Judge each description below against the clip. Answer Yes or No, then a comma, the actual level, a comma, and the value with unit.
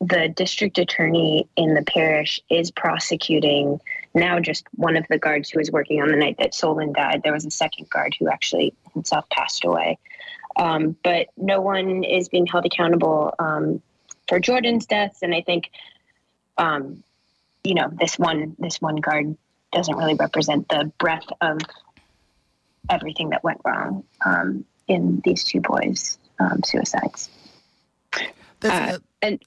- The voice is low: No, medium, 165 Hz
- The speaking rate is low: No, average, 155 wpm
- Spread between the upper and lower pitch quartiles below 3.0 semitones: Yes, narrow, 2.5 semitones